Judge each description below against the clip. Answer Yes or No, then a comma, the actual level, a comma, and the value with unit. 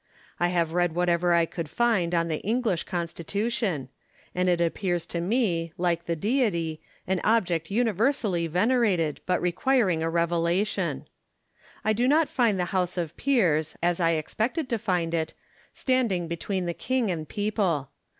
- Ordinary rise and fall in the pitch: Yes, average, 4.4 semitones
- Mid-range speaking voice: Yes, medium, 180 Hz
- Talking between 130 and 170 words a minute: Yes, average, 155 wpm